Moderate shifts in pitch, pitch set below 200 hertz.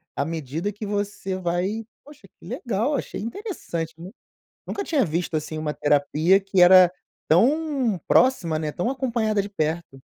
No: wide, 6.2 semitones; high, 190 Hz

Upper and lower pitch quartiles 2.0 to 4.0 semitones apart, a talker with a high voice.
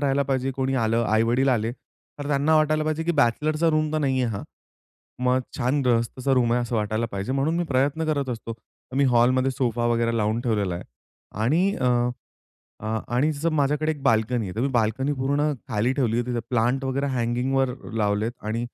No: average, 3.3 semitones; low, 130 Hz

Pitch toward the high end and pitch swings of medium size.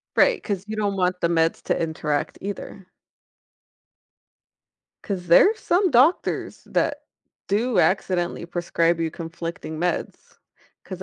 No: medium, 180 Hz; average, 3.4 semitones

